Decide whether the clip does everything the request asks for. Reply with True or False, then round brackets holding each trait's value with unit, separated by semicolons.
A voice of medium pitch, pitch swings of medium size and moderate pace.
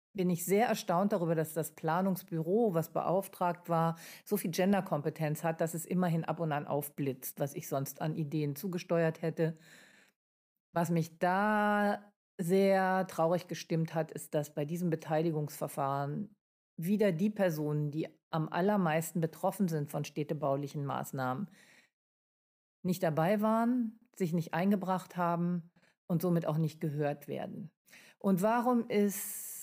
True (170 Hz; 3.6 semitones; 140 wpm)